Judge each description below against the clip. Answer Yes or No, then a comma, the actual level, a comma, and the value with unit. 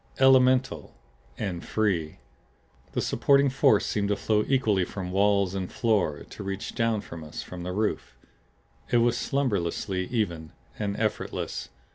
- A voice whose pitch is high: No, low, 105 Hz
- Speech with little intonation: No, average, 4.2 semitones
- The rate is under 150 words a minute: Yes, average, 140 wpm